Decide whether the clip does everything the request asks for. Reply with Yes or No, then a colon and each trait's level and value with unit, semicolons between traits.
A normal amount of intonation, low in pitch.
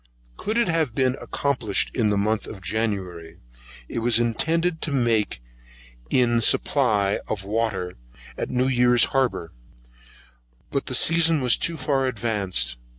Yes: average, 4.7 semitones; low, 120 Hz